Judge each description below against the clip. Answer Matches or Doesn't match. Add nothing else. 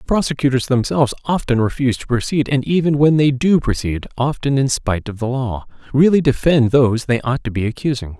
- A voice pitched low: Matches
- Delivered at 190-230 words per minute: Matches